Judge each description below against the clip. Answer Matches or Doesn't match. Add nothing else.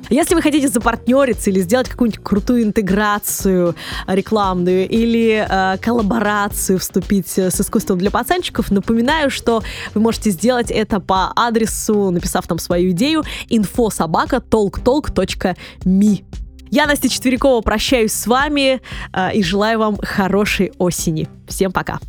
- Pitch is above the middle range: Matches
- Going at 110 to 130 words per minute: Matches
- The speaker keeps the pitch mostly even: Doesn't match